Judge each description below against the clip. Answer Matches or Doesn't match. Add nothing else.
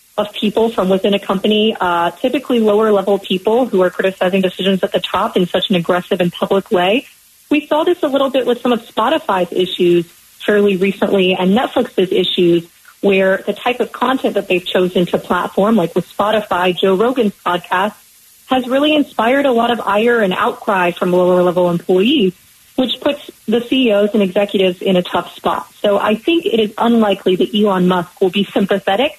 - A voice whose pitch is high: Matches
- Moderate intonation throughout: Matches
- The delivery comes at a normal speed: Matches